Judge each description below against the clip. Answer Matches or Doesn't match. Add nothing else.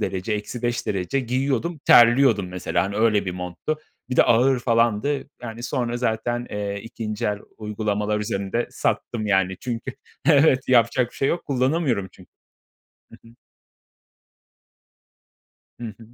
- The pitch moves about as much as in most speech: Matches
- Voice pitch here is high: Doesn't match